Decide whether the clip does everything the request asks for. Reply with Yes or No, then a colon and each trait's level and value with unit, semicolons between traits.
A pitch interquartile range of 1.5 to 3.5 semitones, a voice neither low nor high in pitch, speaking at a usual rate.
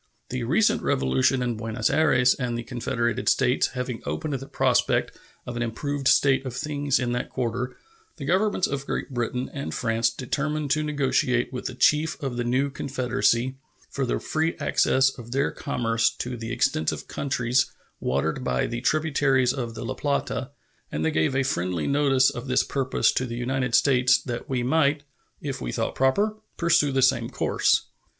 No: narrow, 2.6 semitones; low, 130 Hz; average, 175 wpm